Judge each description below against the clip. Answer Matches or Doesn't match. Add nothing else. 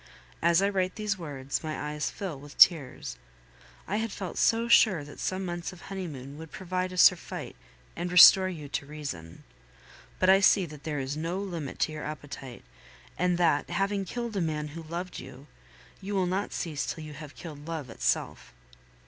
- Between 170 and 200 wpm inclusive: Matches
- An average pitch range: Matches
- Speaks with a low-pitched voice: Doesn't match